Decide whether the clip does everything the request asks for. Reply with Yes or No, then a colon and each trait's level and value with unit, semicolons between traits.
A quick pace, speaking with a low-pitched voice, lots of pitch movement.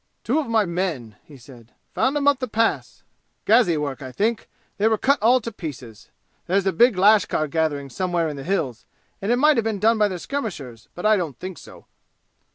No: fast, 210 wpm; high, 190 Hz; wide, 7.3 semitones